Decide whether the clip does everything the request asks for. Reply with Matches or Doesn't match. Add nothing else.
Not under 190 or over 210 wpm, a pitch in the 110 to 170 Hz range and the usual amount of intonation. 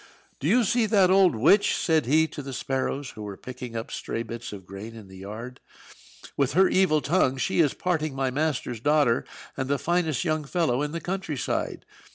Doesn't match